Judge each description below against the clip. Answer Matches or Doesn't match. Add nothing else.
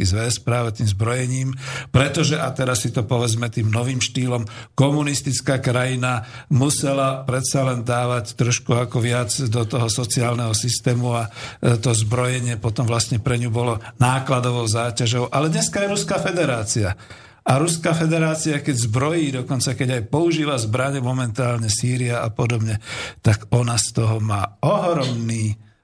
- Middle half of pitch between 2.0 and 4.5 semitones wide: Matches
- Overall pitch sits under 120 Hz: Doesn't match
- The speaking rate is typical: Matches